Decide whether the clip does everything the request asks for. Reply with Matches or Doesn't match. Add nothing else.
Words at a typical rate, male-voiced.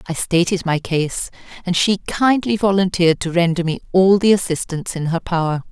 Doesn't match